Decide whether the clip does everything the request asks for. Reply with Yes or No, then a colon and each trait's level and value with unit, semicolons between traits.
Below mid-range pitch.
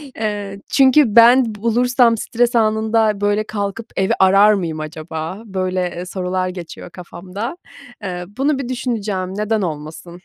No: high, 205 Hz